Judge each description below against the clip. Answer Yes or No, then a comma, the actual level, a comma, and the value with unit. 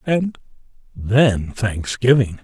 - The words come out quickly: No, slow, 75 wpm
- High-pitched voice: No, low, 115 Hz